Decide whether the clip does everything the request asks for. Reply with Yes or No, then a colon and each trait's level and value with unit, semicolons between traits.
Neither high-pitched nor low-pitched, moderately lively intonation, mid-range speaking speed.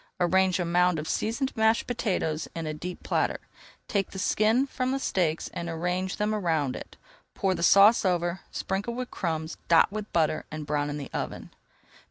Yes: medium, 180 Hz; average, 4.6 semitones; average, 185 wpm